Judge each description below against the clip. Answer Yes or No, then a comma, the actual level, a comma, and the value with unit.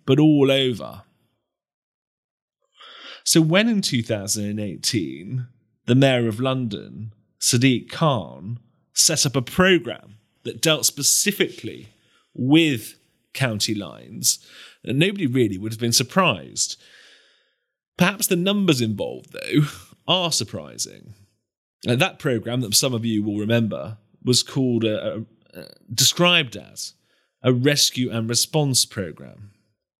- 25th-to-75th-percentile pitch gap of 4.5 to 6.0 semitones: Yes, average, 5.0 semitones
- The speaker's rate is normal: No, slow, 115 wpm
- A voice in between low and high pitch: No, low, 125 Hz